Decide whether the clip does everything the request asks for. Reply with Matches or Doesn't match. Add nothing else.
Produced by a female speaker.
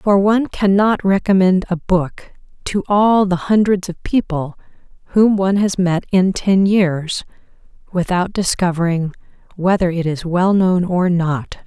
Matches